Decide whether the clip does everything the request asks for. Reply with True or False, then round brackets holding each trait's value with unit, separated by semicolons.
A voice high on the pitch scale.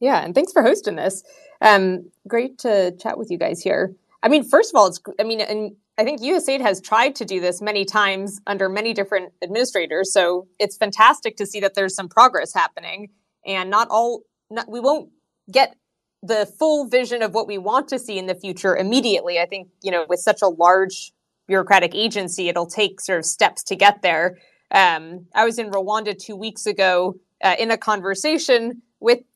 True (205 Hz)